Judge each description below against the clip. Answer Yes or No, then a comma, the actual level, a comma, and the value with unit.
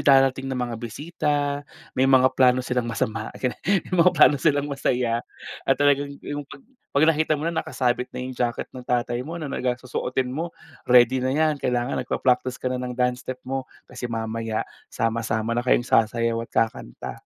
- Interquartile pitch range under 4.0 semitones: Yes, narrow, 2.6 semitones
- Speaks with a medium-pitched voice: No, low, 125 Hz